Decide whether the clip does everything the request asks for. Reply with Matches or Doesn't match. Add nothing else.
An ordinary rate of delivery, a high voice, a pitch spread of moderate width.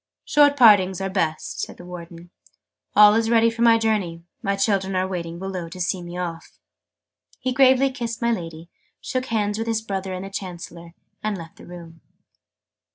Matches